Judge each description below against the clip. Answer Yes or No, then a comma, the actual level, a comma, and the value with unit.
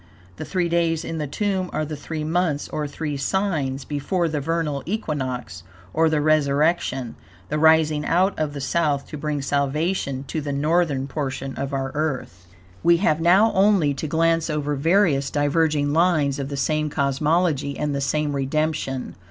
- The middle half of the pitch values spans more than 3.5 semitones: No, average, 2.8 semitones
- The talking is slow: No, average, 170 wpm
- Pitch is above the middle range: No, medium, 150 Hz